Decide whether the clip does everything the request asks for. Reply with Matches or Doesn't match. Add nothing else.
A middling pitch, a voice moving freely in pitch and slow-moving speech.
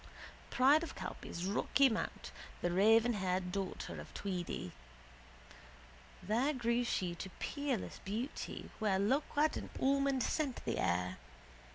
Doesn't match